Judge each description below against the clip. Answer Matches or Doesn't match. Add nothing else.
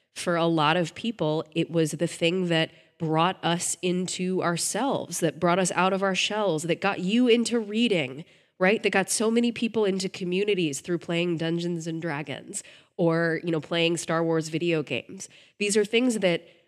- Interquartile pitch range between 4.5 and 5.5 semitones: Doesn't match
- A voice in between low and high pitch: Matches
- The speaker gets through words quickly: Doesn't match